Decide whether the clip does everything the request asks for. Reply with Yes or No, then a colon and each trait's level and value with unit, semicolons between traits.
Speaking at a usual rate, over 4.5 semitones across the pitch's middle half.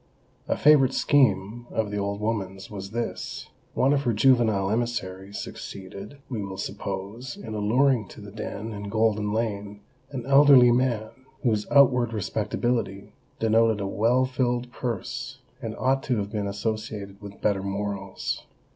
No: average, 145 wpm; average, 3.4 semitones